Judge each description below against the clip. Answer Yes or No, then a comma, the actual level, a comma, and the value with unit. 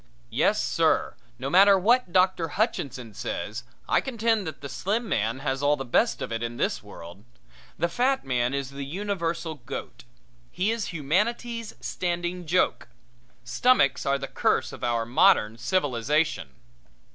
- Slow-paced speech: No, average, 150 wpm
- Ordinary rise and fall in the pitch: No, wide, 7.8 semitones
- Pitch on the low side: No, medium, 155 Hz